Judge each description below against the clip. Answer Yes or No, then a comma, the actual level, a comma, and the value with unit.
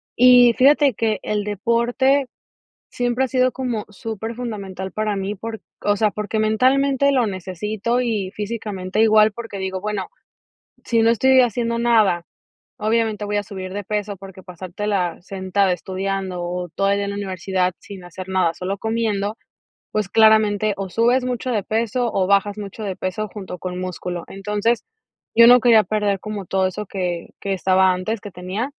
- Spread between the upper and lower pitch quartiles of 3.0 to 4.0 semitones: Yes, average, 3.3 semitones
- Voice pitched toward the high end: Yes, high, 210 Hz